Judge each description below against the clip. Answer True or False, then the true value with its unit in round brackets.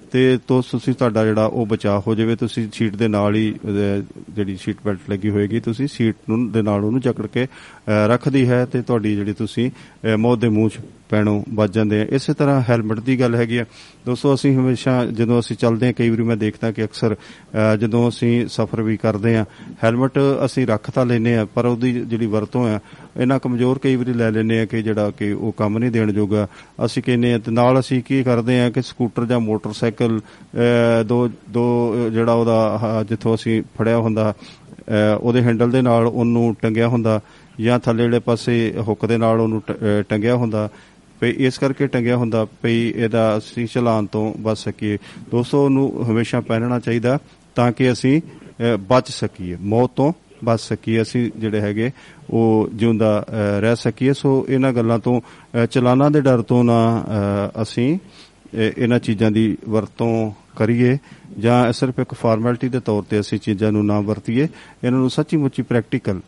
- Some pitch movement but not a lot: False (2.2 semitones)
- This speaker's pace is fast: True (170 wpm)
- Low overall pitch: True (115 Hz)